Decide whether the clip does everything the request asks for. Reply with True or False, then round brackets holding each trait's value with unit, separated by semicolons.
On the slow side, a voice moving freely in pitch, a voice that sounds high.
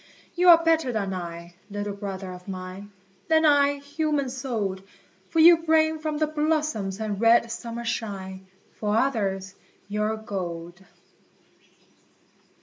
True (130 wpm; 7.7 semitones; 220 Hz)